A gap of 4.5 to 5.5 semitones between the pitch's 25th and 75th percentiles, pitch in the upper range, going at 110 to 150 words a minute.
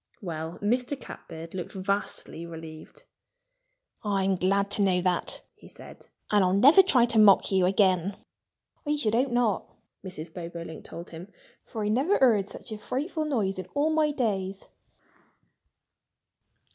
Yes: average, 5.0 semitones; high, 200 Hz; average, 145 wpm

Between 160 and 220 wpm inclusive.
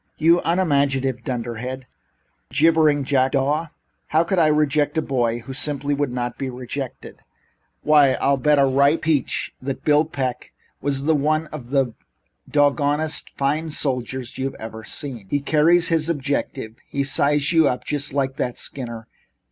No: average, 150 wpm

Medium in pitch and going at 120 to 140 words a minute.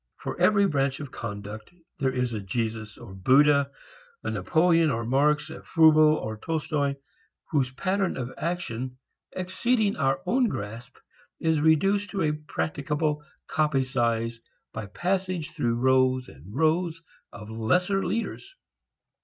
Yes: medium, 145 Hz; slow, 135 wpm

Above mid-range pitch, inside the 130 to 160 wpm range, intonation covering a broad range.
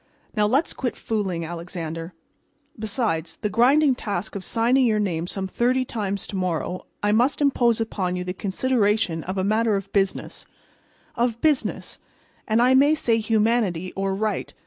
No: high, 210 Hz; average, 155 wpm; average, 4.2 semitones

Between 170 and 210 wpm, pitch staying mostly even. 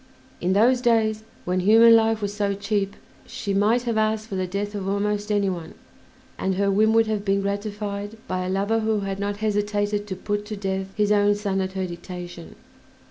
Yes: average, 200 wpm; narrow, 1.7 semitones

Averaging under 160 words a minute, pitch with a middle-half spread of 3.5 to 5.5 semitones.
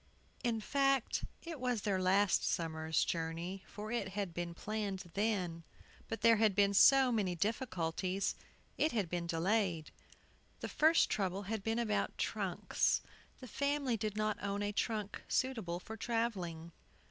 Yes: average, 145 wpm; average, 4.0 semitones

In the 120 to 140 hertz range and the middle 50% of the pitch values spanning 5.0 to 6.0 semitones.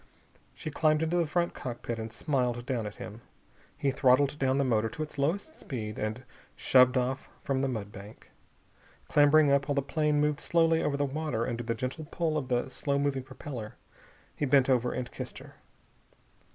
No: low, 135 Hz; average, 3.5 semitones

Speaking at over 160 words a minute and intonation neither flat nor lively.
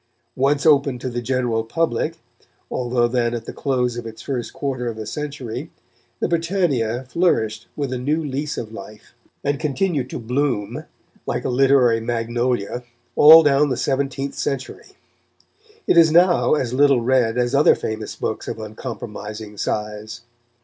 No: average, 155 wpm; average, 3.7 semitones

